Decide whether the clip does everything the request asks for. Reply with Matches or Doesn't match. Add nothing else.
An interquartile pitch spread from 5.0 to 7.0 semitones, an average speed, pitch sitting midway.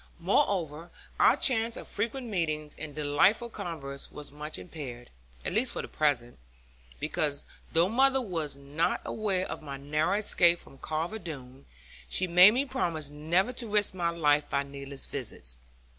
Matches